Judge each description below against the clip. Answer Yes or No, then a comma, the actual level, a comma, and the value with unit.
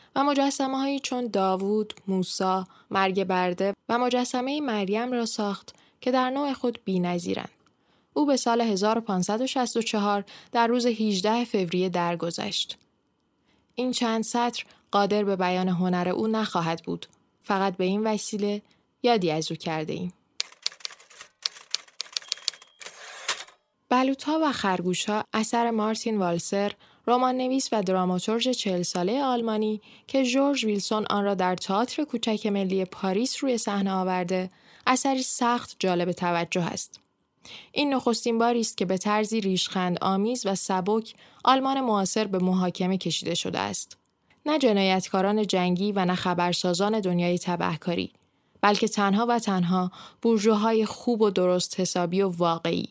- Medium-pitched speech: No, high, 205 Hz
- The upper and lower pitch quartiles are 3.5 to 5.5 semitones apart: Yes, average, 4.4 semitones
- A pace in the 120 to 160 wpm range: Yes, average, 130 wpm